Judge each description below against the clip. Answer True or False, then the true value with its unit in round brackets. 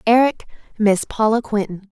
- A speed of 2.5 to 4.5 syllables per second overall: False (4.8 syllables/s)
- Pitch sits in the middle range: False (215 Hz)